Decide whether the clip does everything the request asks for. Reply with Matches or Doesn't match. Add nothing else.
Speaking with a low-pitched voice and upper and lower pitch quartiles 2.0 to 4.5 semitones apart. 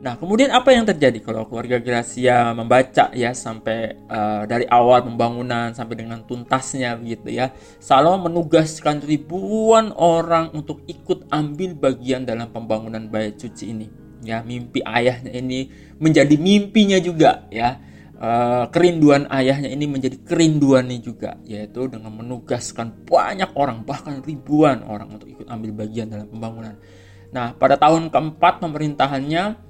Doesn't match